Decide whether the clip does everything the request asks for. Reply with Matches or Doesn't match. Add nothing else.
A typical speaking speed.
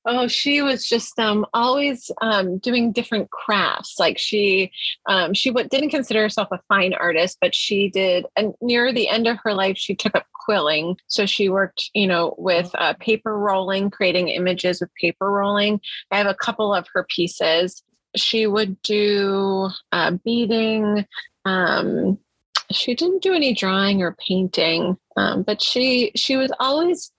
Matches